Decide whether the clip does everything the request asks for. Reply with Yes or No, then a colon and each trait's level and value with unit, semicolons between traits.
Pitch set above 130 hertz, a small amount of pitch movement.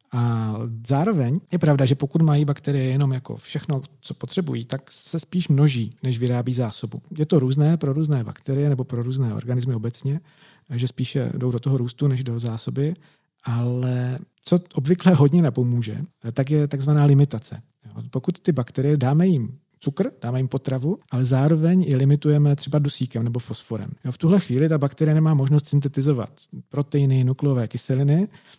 No: medium, 140 Hz; average, 3.2 semitones